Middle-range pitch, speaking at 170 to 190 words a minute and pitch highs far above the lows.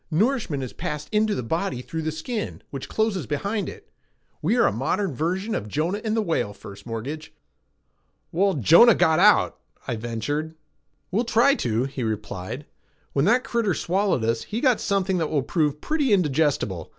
Yes: medium, 160 Hz; average, 175 wpm; wide, 7.8 semitones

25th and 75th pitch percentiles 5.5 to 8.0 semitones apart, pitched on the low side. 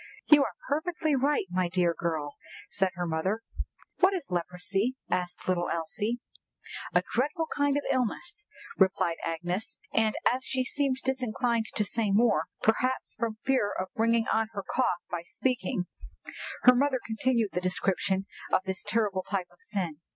No: wide, 6.0 semitones; high, 215 Hz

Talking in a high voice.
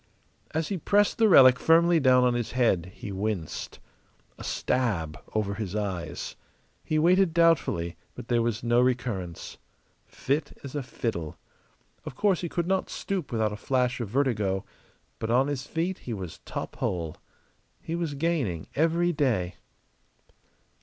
No: low, 125 Hz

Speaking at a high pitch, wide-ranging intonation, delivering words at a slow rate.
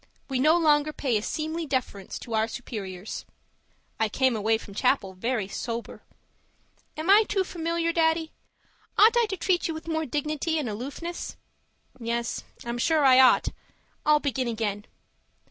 No: very high, 275 Hz; wide, 5.9 semitones; average, 155 wpm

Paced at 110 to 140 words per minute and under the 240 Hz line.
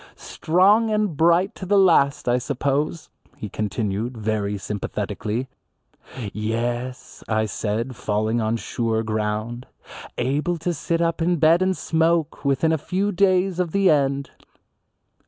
Yes: slow, 135 wpm; medium, 140 Hz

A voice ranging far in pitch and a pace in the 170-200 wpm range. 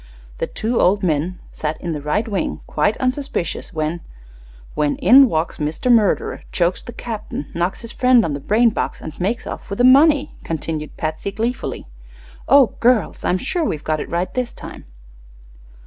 Yes: wide, 7.4 semitones; average, 180 wpm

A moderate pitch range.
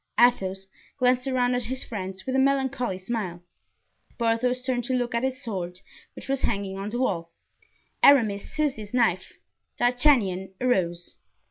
Yes: average, 4.9 semitones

